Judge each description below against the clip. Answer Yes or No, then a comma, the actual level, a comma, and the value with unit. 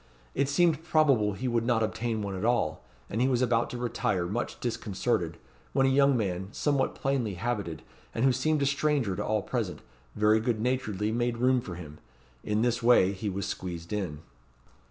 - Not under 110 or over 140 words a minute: No, average, 190 wpm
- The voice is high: No, low, 115 Hz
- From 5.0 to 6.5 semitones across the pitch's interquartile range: No, average, 4.5 semitones